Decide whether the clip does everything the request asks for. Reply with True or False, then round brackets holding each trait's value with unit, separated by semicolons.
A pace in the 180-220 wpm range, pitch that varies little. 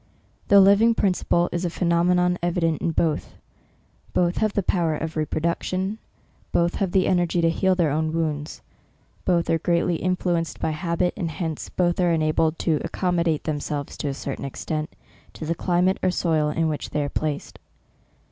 True (185 wpm; 2.3 semitones)